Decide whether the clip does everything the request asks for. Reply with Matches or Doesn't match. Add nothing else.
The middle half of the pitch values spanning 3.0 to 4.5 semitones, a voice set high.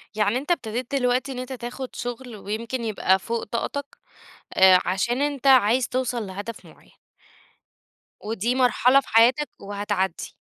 Matches